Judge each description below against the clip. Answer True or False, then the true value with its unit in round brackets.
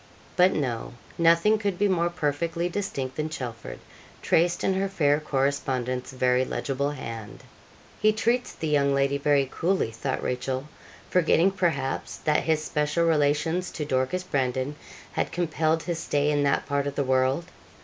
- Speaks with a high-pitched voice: False (150 Hz)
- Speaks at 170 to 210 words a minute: False (155 wpm)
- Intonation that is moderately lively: True (4.2 semitones)